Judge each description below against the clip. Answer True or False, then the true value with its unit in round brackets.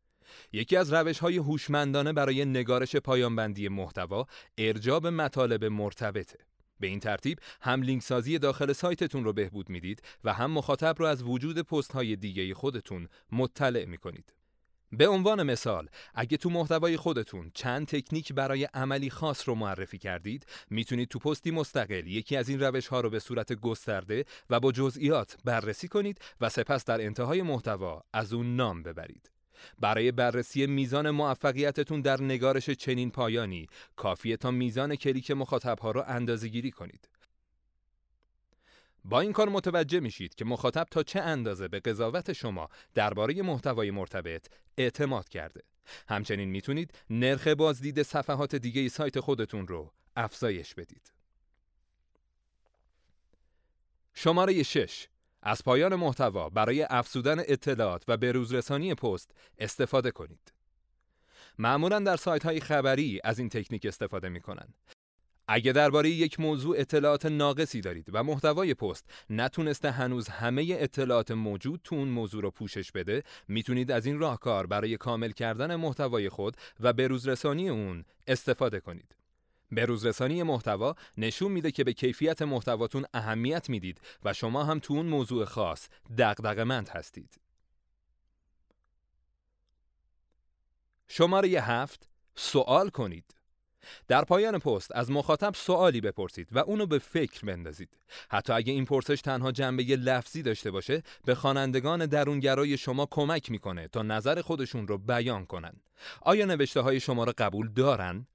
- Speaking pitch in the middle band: False (125 Hz)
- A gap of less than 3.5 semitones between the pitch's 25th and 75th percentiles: False (5.2 semitones)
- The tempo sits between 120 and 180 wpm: True (140 wpm)